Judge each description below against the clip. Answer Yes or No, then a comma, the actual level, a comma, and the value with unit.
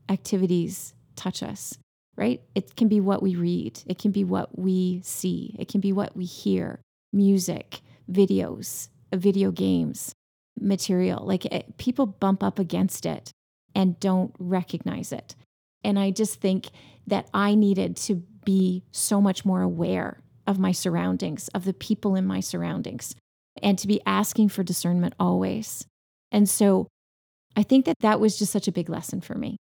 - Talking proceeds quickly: No, average, 165 wpm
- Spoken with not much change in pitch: Yes, narrow, 2.3 semitones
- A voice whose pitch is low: No, high, 190 Hz